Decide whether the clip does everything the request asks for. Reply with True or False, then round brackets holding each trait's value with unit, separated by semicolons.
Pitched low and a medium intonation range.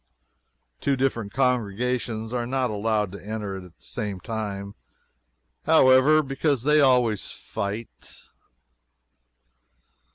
True (115 Hz; 4.2 semitones)